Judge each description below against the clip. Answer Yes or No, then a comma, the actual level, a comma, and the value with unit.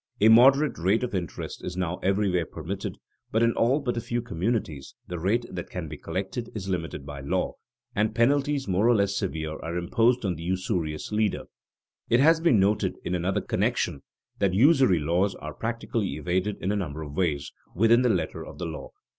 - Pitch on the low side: Yes, low, 100 Hz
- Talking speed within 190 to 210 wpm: Yes, average, 195 wpm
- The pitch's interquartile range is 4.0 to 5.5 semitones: Yes, average, 5.1 semitones